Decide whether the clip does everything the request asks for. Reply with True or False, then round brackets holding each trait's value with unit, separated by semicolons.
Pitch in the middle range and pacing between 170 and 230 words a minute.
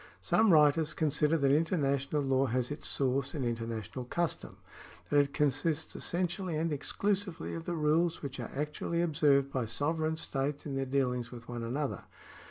True (145 Hz; 175 wpm)